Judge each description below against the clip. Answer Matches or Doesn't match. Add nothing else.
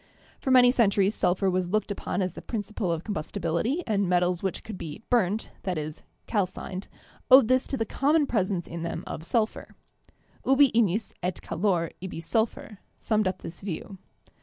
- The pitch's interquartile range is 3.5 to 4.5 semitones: Matches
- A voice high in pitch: Matches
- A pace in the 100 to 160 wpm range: Doesn't match